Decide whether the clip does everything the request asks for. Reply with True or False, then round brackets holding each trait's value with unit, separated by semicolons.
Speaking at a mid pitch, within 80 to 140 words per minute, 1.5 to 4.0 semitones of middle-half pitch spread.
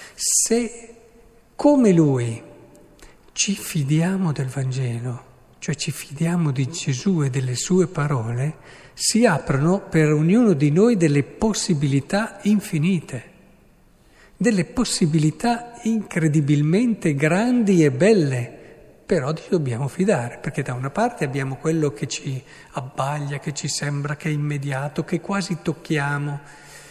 False (155 Hz; 120 wpm; 5.5 semitones)